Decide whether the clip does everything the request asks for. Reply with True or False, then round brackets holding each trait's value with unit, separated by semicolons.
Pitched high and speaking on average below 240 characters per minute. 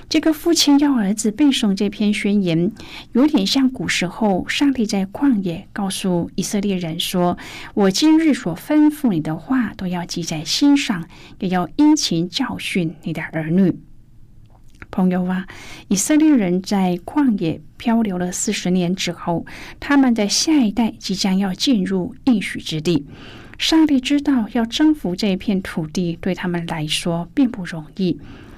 True (195 Hz; 230 characters per minute)